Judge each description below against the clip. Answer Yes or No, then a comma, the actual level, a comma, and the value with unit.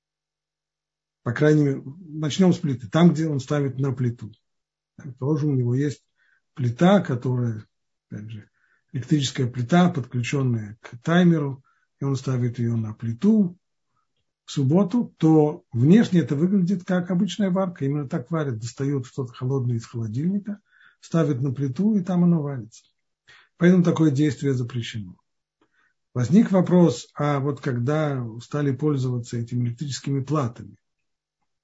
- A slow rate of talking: No, average, 135 wpm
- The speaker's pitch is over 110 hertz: Yes, medium, 140 Hz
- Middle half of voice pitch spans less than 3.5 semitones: No, average, 5.3 semitones